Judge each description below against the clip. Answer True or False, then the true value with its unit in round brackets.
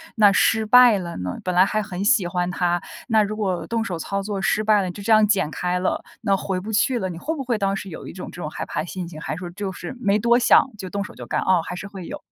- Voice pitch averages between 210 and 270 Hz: False (195 Hz)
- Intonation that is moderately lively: True (3.2 semitones)